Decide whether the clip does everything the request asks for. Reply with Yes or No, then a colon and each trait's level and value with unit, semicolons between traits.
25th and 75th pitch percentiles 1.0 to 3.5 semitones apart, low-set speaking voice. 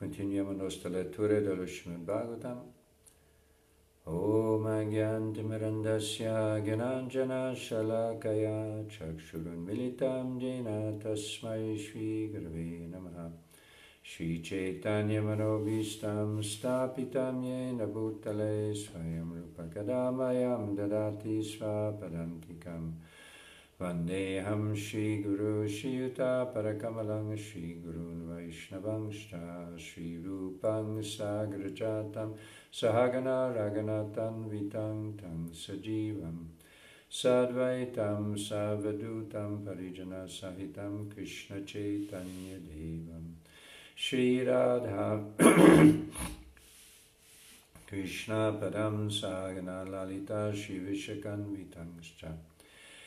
Yes: average, 3.1 semitones; low, 105 Hz